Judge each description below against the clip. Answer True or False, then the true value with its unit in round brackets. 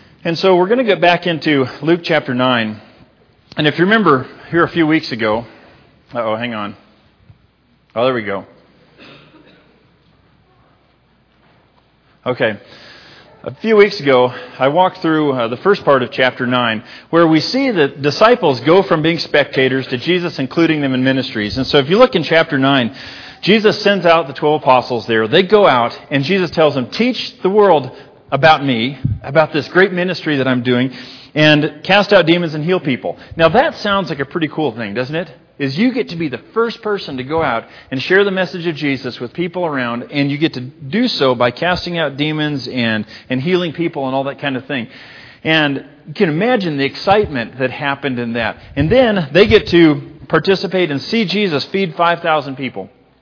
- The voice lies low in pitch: False (150 Hz)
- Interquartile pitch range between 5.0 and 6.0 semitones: True (5.4 semitones)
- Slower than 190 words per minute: False (195 wpm)